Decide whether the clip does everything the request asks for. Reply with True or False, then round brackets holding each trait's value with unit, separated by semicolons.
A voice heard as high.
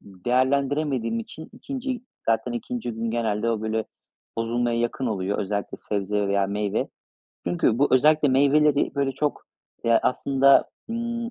False (120 Hz)